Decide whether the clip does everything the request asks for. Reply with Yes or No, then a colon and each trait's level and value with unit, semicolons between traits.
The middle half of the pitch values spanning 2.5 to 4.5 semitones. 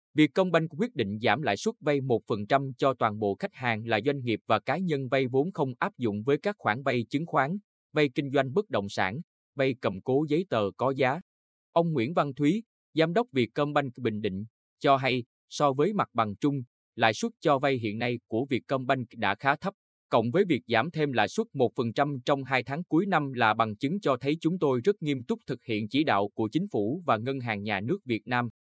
No: average, 5.0 semitones